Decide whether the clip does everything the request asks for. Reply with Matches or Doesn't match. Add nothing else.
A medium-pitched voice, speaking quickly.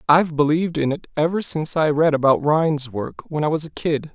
Matches